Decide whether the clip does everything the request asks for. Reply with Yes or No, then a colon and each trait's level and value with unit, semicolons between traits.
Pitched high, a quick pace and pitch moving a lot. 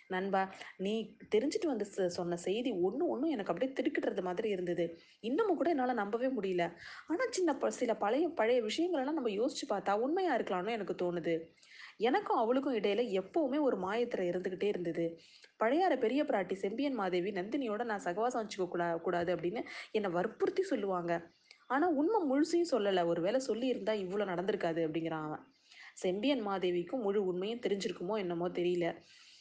Yes: high, 210 Hz; fast, 150 wpm; wide, 6.9 semitones